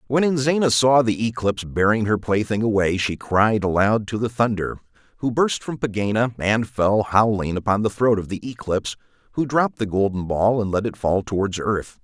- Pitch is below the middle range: Yes, low, 110 Hz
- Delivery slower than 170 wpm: No, average, 195 wpm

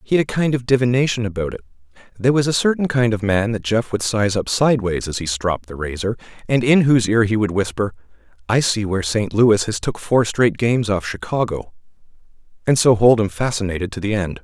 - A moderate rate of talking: No, fast, 215 wpm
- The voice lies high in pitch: No, low, 110 Hz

